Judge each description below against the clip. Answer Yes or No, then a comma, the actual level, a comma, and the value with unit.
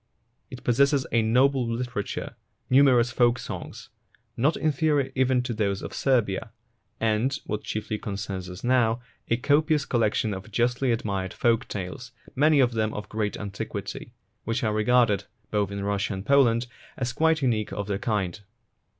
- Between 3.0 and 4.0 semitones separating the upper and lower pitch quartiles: Yes, average, 3.7 semitones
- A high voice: No, low, 115 Hz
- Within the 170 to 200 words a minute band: No, average, 160 wpm